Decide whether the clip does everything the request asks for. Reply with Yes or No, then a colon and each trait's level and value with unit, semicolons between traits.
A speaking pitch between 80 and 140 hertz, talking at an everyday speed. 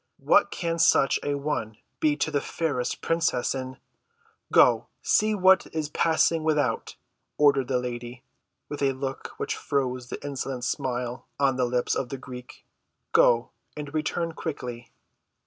Yes: low, 135 Hz; average, 145 wpm